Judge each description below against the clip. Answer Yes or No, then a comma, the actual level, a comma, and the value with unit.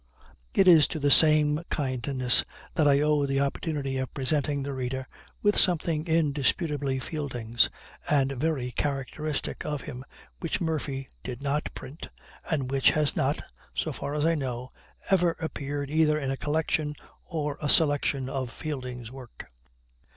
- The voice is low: No, medium, 145 Hz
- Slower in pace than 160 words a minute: Yes, average, 150 wpm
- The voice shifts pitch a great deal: No, narrow, 2.5 semitones